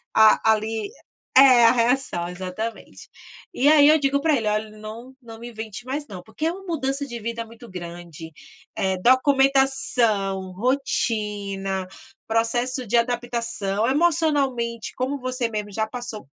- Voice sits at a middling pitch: No, high, 235 Hz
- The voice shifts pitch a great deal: No, average, 4.0 semitones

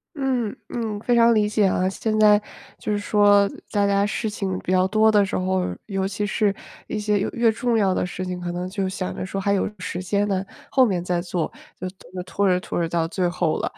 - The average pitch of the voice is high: Yes, high, 200 Hz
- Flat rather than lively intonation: Yes, narrow, 2.3 semitones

